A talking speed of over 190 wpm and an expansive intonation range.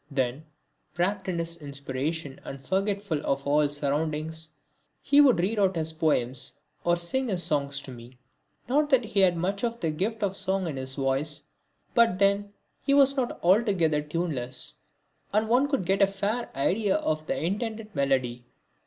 No: average, 170 wpm; wide, 6.1 semitones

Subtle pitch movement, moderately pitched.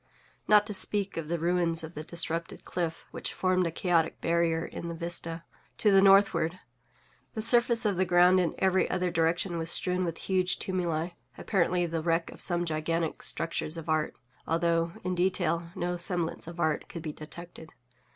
Yes: narrow, 1.8 semitones; medium, 170 Hz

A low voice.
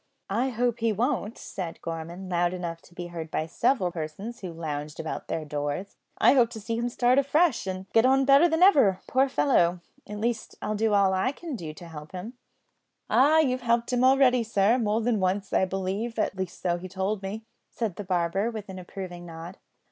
No: high, 200 Hz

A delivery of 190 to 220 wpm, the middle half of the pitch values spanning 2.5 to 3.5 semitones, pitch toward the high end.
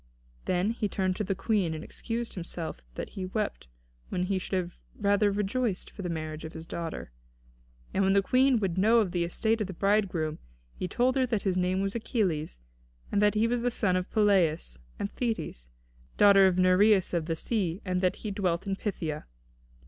Yes: average, 200 wpm; average, 3.2 semitones; high, 195 Hz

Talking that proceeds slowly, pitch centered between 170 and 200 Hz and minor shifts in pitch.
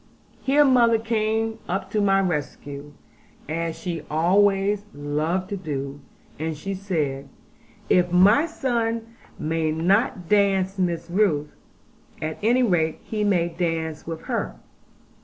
No: slow, 125 wpm; medium, 185 Hz; average, 4.7 semitones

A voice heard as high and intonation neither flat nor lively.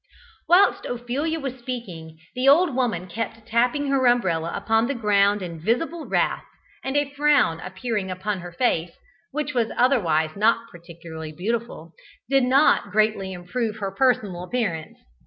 No: high, 225 Hz; wide, 6.2 semitones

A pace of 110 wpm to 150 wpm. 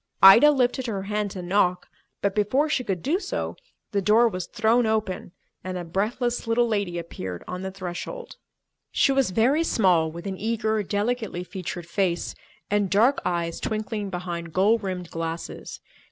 No: average, 165 wpm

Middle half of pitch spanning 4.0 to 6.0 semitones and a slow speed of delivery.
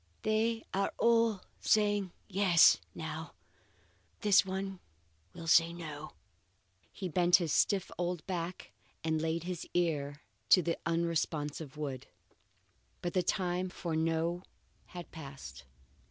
No: average, 2.9 semitones; slow, 125 wpm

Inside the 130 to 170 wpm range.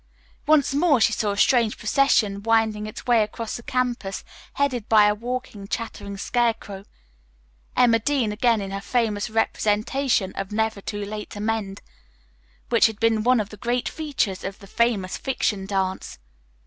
Yes: average, 160 wpm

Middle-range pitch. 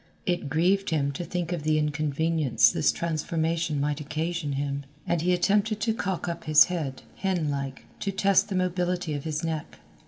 Yes: medium, 160 Hz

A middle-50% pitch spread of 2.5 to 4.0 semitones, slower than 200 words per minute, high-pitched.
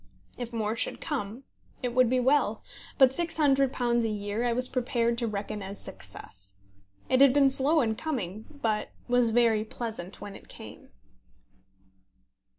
Yes: average, 3.5 semitones; average, 155 wpm; high, 235 Hz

